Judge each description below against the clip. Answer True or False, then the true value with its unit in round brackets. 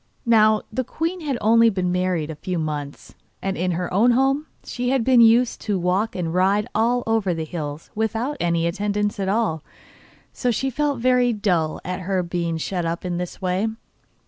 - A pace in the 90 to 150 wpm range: False (190 wpm)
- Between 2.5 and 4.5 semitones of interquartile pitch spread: False (4.9 semitones)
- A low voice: False (200 Hz)